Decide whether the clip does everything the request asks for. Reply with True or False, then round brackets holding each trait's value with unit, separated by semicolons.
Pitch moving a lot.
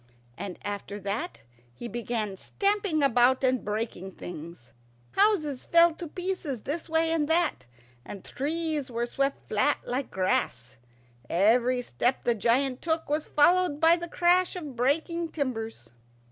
True (6.7 semitones)